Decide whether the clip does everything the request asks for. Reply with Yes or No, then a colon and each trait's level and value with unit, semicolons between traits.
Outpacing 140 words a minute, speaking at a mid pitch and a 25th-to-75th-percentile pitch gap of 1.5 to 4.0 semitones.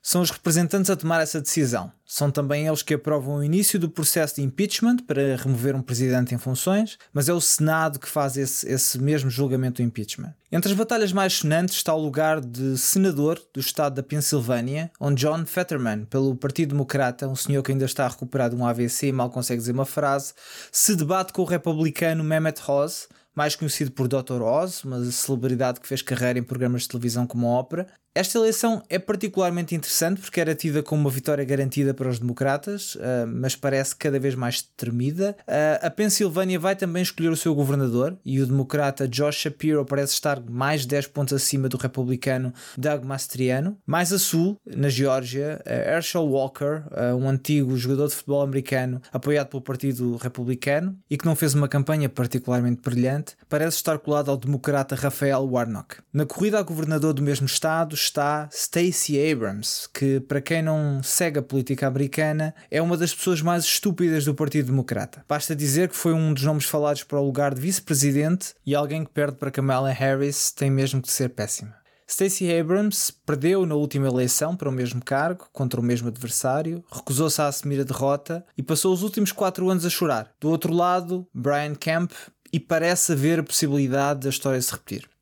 Yes: fast, 185 wpm; medium, 145 Hz; average, 3.5 semitones